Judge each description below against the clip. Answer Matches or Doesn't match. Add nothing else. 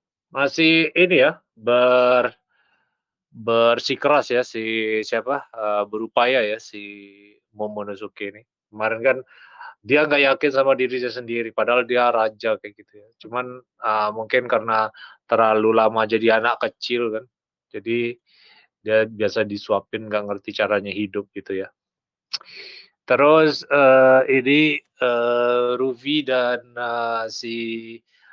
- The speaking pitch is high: Doesn't match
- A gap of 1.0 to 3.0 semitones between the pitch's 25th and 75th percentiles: Matches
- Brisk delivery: Doesn't match